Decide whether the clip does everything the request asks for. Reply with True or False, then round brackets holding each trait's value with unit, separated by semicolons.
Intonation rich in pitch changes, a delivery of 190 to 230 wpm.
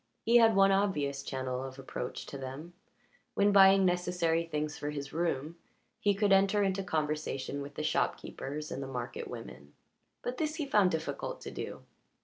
False (5.9 semitones; 175 wpm)